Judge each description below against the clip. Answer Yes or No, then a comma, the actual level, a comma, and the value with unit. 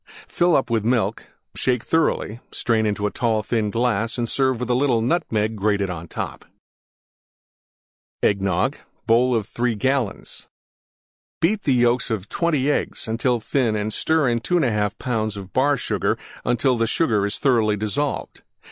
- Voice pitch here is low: Yes, low, 115 Hz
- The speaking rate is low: No, average, 145 wpm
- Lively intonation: No, average, 3.4 semitones